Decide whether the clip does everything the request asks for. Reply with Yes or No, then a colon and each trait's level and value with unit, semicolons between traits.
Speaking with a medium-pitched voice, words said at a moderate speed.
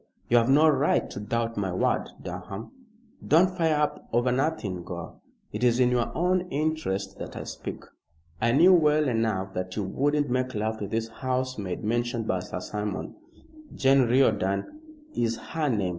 No: low, 120 Hz; average, 170 wpm